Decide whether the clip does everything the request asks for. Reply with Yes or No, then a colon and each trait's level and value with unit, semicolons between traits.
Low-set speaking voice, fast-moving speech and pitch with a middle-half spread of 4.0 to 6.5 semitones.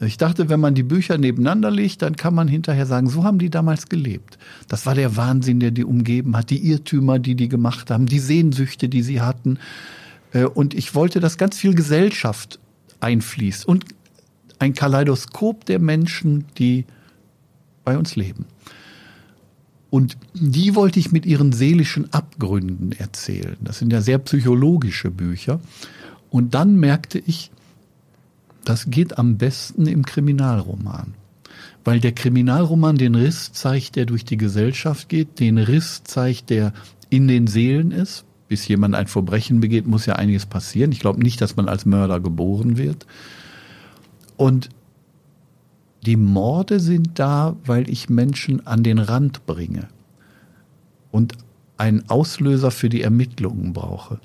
No: low, 130 Hz; average, 150 wpm; average, 5.1 semitones